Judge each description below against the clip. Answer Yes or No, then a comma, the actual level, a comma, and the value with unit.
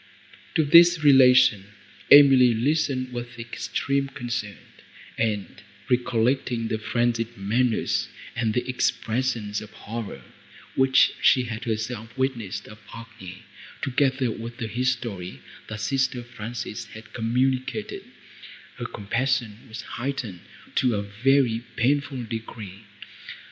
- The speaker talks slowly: Yes, slow, 110 wpm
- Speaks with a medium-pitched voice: No, low, 120 Hz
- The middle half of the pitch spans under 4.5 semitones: Yes, average, 2.9 semitones